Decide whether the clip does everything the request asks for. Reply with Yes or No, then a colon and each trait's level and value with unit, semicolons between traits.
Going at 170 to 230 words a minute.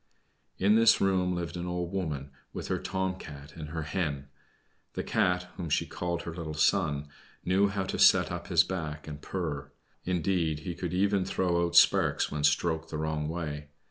Yes: average, 185 wpm